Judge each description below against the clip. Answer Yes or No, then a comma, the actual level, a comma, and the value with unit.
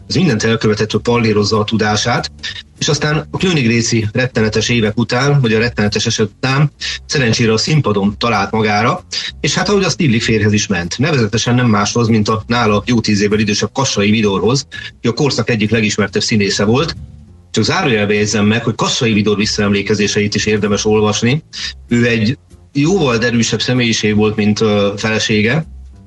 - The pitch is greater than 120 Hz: No, low, 110 Hz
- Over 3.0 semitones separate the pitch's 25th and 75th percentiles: No, narrow, 2.5 semitones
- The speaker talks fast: Yes, fast, 165 wpm